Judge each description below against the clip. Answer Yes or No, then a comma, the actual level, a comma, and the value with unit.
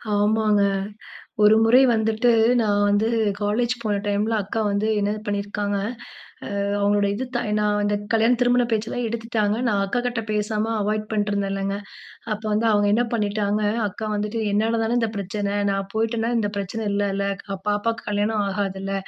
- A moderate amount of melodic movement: No, narrow, 1.7 semitones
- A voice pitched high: Yes, high, 210 Hz